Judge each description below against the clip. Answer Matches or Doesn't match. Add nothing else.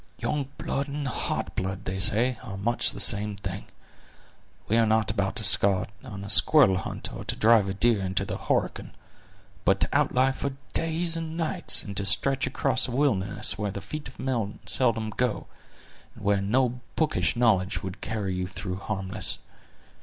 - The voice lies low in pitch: Matches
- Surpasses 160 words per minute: Matches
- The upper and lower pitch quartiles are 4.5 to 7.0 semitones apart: Matches